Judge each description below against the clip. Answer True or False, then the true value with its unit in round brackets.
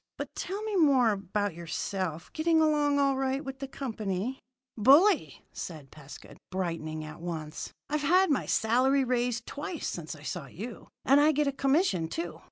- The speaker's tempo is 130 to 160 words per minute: False (170 wpm)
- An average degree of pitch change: False (8.7 semitones)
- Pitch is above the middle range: True (250 Hz)